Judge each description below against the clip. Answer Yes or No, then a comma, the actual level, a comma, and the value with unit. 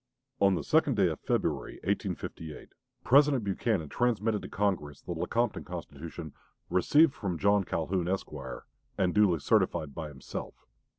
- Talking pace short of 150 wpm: Yes, slow, 135 wpm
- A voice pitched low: Yes, very low, 95 Hz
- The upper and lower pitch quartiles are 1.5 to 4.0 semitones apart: No, average, 4.7 semitones